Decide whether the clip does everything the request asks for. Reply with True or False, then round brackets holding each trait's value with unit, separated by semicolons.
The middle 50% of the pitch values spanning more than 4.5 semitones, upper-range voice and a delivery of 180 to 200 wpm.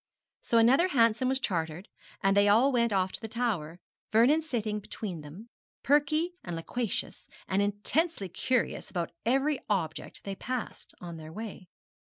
False (5.4 semitones; 215 Hz; 155 wpm)